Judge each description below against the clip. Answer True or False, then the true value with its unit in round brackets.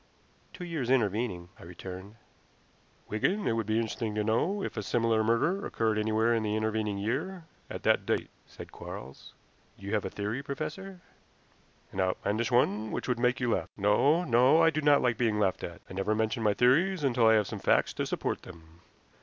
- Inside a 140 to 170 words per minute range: False (195 wpm)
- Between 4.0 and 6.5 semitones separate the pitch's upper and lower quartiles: True (4.3 semitones)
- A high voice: False (115 Hz)